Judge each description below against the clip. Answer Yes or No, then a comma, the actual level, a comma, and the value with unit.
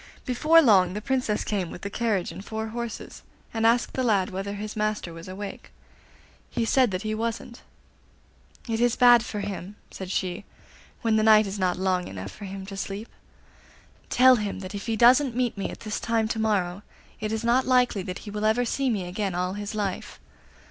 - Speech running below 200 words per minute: No, fast, 205 wpm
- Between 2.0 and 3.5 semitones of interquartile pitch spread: Yes, average, 3.2 semitones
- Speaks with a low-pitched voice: No, high, 215 Hz